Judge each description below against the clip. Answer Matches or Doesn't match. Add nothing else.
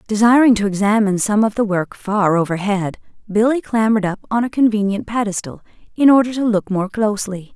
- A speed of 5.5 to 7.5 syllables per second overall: Matches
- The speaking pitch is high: Matches